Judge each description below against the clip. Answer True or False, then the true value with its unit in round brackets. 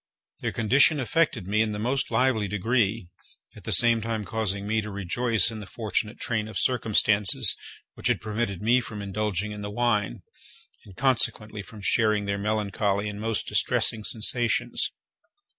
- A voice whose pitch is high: False (110 Hz)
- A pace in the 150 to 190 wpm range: True (160 wpm)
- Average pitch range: False (2.0 semitones)